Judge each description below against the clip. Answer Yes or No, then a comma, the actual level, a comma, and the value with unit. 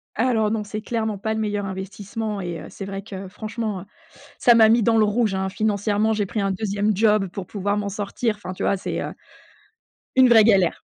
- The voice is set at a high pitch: Yes, high, 210 Hz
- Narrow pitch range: Yes, narrow, 2.0 semitones